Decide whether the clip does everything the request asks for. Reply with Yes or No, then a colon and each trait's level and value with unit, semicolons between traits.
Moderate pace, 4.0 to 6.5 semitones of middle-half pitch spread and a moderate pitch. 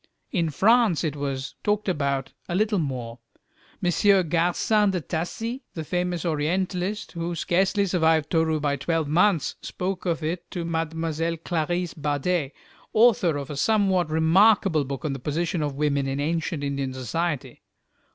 No: average, 150 wpm; average, 3.6 semitones; medium, 165 Hz